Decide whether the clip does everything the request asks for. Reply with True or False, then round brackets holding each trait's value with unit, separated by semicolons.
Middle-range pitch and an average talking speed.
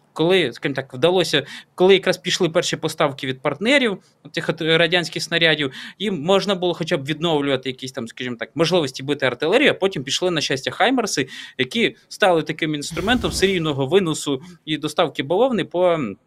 False (165 Hz; 160 wpm)